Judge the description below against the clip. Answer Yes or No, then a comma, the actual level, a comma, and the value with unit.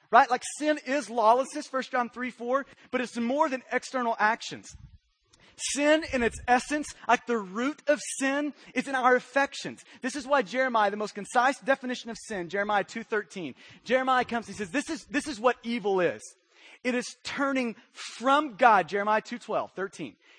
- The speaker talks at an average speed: Yes, average, 180 wpm